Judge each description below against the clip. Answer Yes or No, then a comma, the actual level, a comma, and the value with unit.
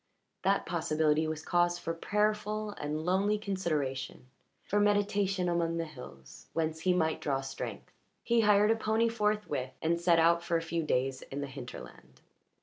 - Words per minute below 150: No, average, 160 wpm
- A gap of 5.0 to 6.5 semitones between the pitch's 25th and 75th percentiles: Yes, wide, 5.4 semitones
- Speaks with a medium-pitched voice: Yes, medium, 170 Hz